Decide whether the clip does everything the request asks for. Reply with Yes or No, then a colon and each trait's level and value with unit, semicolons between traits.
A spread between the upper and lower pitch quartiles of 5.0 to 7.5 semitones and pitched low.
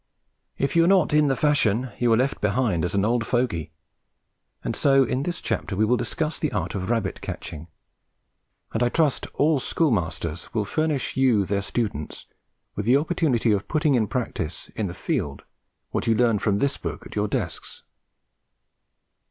Yes: wide, 5.6 semitones; low, 120 Hz